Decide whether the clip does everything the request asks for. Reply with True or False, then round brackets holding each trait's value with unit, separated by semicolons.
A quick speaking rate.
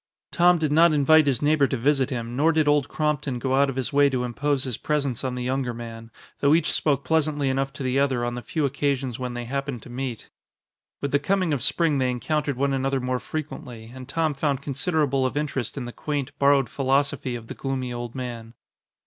True (220 wpm)